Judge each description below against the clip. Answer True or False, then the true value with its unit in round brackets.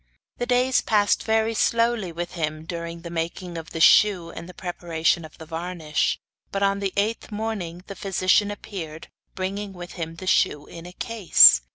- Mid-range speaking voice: True (180 Hz)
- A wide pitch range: False (3.7 semitones)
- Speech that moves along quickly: False (180 wpm)